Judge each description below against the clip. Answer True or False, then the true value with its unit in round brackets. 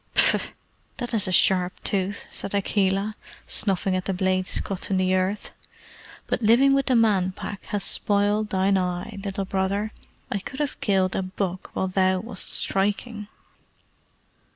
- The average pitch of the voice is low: False (195 Hz)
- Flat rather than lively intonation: True (1.9 semitones)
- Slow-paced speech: False (155 wpm)